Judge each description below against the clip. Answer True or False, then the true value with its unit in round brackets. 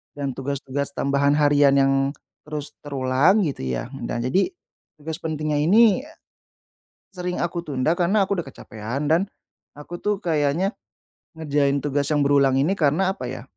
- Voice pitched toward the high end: False (145 Hz)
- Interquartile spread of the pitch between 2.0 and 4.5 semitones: True (3.9 semitones)